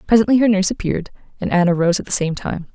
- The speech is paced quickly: Yes, fast, 240 wpm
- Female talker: Yes, female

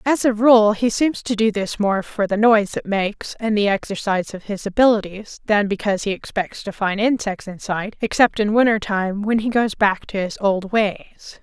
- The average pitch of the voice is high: Yes, high, 210 Hz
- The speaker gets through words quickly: Yes, fast, 210 wpm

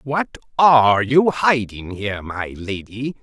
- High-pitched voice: No, low, 120 Hz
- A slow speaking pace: Yes, slow, 130 wpm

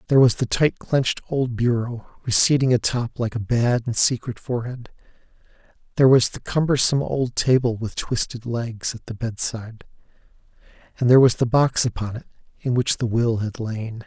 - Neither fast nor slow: Yes, average, 175 wpm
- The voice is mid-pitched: No, low, 120 Hz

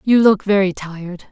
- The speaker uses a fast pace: No, average, 185 wpm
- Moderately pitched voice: No, high, 195 Hz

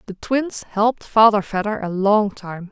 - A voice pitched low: No, high, 205 Hz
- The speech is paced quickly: No, average, 175 wpm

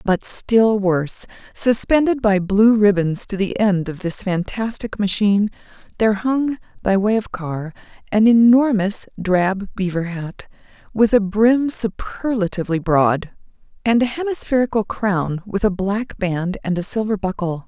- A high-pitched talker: Yes, high, 205 Hz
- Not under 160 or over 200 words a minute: No, average, 145 wpm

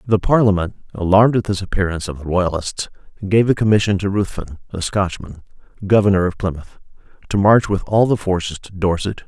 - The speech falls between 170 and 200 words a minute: Yes, average, 175 wpm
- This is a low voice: Yes, very low, 95 Hz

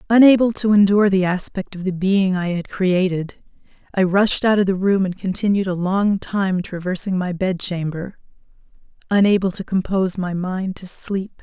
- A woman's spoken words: Yes, female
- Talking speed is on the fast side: No, average, 175 wpm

